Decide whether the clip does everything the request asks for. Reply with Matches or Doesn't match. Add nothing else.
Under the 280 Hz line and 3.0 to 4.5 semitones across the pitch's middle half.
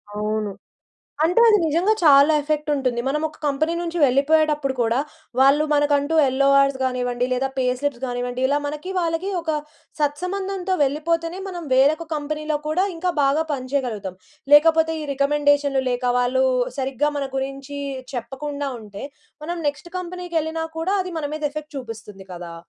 Doesn't match